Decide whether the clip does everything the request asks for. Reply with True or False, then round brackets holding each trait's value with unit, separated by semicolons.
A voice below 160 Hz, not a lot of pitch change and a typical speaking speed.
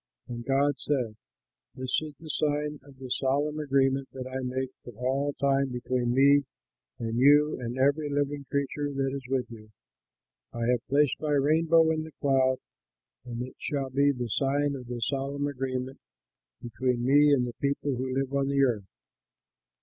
True (135 Hz; 2.1 semitones; 170 wpm)